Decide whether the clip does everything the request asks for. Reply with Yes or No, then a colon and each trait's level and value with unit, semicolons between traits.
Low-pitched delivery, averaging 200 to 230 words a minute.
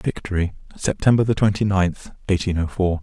No: very low, 95 Hz; average, 140 wpm